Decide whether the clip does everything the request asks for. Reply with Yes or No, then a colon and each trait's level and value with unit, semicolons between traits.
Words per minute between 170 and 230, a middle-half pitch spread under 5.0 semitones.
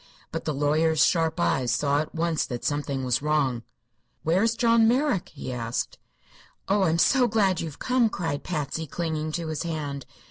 Yes: average, 175 wpm; average, 4.5 semitones